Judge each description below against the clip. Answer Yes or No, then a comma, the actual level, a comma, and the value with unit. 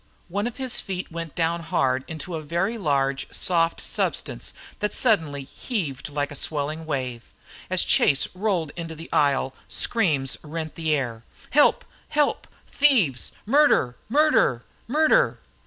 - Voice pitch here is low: No, medium, 165 Hz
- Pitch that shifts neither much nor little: No, wide, 6.6 semitones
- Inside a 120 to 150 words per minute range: Yes, average, 140 wpm